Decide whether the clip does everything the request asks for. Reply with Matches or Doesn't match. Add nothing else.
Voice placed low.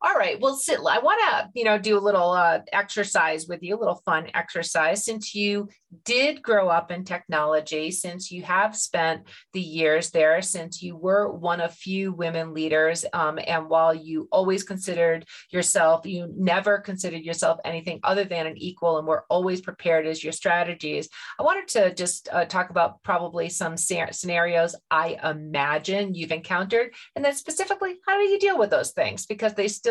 Doesn't match